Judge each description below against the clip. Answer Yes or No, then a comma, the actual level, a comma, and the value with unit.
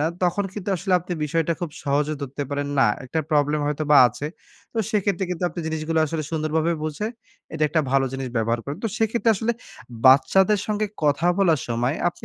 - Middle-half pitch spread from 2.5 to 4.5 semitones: Yes, average, 4.2 semitones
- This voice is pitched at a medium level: Yes, medium, 155 Hz